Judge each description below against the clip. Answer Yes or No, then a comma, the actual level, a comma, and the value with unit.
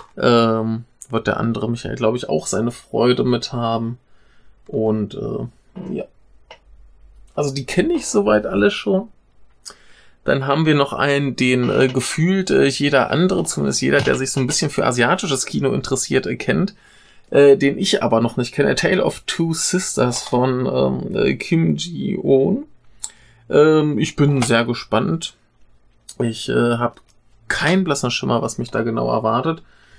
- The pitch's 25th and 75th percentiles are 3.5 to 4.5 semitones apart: Yes, average, 4.0 semitones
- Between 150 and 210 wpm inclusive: Yes, average, 155 wpm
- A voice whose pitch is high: No, low, 125 Hz